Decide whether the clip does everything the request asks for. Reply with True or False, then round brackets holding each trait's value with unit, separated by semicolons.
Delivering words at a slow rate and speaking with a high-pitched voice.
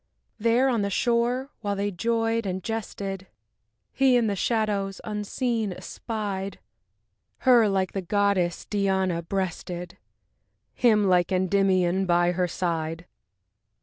True (115 wpm; 200 Hz)